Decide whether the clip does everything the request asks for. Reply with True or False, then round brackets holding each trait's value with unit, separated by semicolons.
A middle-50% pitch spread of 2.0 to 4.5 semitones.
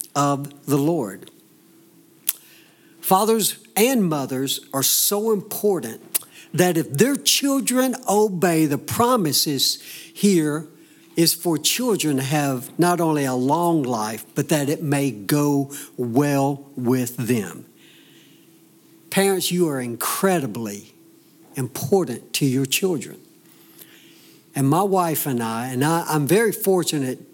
False (5.1 semitones)